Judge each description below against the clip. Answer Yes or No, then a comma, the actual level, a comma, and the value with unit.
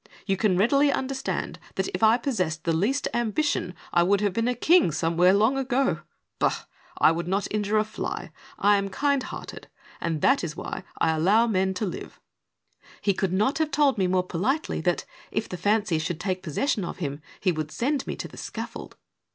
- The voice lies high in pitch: Yes, high, 200 Hz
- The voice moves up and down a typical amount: No, wide, 6.0 semitones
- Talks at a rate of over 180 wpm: Yes, average, 200 wpm